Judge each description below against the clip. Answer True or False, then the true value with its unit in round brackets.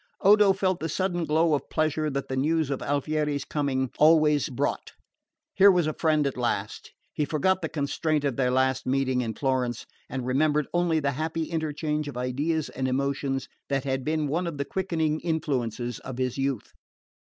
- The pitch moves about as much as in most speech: True (3.2 semitones)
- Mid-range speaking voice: True (145 Hz)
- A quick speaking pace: False (180 wpm)